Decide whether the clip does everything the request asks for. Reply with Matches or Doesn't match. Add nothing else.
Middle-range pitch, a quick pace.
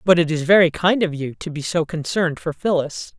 Matches